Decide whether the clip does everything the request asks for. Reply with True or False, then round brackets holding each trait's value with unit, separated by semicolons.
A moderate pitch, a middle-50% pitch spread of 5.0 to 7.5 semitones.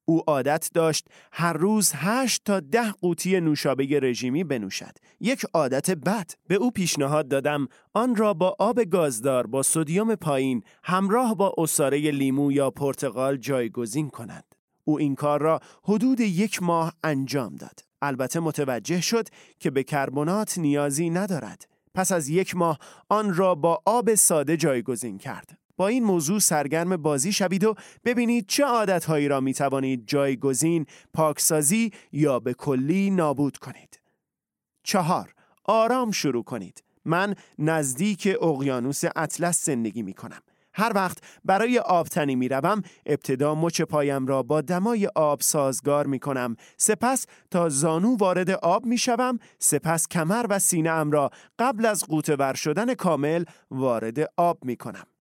True (165 Hz; 5.4 semitones)